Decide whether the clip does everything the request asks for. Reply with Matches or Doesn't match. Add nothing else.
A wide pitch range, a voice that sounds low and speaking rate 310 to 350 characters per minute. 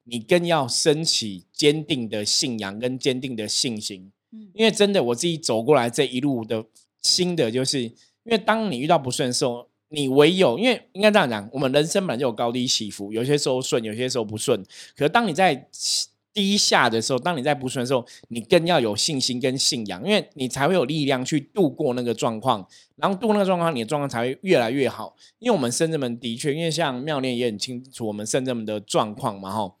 Matches